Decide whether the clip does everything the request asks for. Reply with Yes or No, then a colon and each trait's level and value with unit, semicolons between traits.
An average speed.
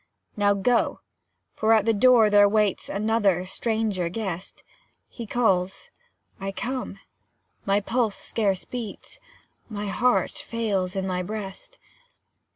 No: slow, 120 wpm